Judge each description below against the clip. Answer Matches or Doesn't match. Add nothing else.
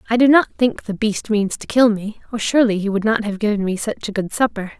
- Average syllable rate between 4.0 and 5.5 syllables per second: Doesn't match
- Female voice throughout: Matches